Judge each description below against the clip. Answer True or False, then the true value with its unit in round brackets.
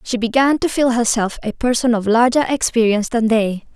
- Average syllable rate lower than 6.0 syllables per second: True (5.4 syllables/s)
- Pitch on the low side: False (235 Hz)